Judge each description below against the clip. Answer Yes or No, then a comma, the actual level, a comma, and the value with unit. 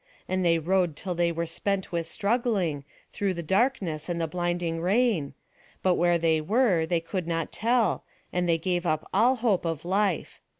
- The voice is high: No, medium, 175 Hz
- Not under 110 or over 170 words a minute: No, average, 180 wpm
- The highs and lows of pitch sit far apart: No, average, 3.2 semitones